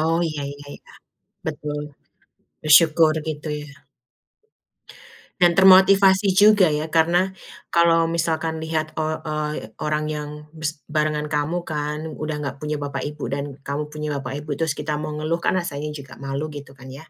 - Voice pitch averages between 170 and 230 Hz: No, medium, 155 Hz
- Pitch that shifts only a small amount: Yes, narrow, 1.8 semitones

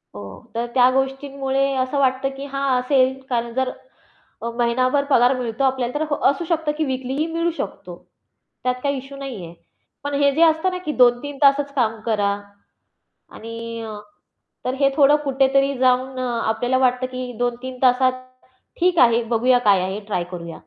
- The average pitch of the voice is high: Yes, very high, 260 Hz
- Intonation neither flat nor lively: No, narrow, 2.3 semitones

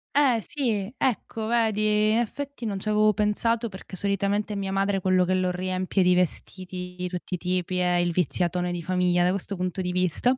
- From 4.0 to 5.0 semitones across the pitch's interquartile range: No, average, 2.8 semitones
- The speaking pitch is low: No, high, 190 Hz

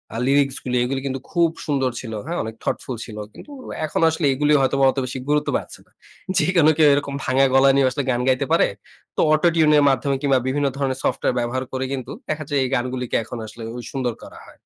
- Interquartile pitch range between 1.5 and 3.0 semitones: Yes, narrow, 2.4 semitones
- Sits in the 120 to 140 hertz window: Yes, low, 135 Hz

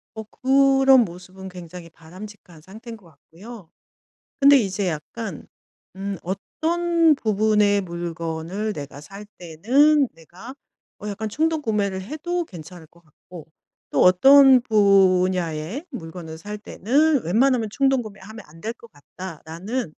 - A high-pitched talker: Yes, high, 200 Hz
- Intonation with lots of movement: Yes, wide, 6.3 semitones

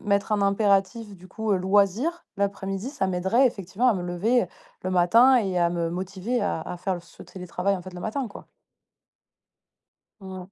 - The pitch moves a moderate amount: Yes, average, 3.2 semitones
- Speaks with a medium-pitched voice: No, high, 195 Hz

